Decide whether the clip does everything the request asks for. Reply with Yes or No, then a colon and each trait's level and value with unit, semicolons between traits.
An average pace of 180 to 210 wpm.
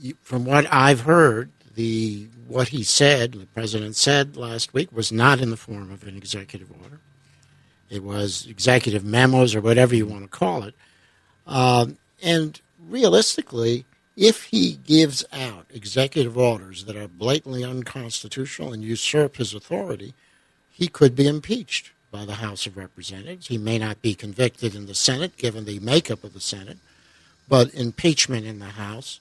No: average, 160 wpm